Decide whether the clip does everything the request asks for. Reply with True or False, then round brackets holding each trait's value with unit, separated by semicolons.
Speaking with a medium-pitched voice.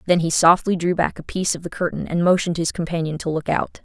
True (170 Hz)